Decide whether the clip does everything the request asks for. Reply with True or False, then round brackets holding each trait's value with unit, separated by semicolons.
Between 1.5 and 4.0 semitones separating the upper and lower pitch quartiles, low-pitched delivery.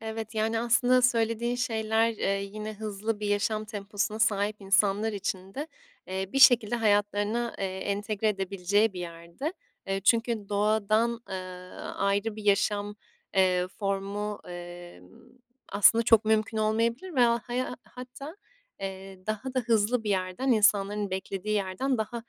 False (2.5 semitones; 210 Hz)